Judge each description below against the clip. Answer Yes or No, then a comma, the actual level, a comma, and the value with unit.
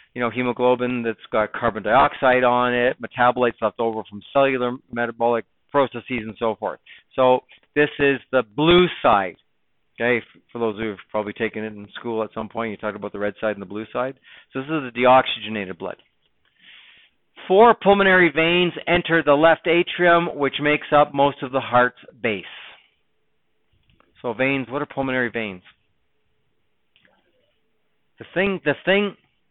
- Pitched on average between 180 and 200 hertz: No, low, 125 Hz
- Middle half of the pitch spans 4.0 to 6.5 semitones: Yes, average, 4.5 semitones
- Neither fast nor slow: Yes, average, 160 wpm